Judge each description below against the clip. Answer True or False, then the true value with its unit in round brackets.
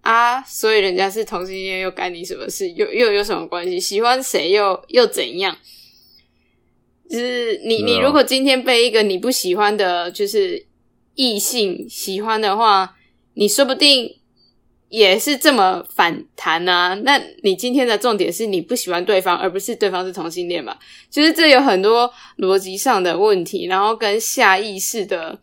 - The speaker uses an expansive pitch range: True (6.6 semitones)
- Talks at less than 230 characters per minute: False (255 characters per minute)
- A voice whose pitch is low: False (230 Hz)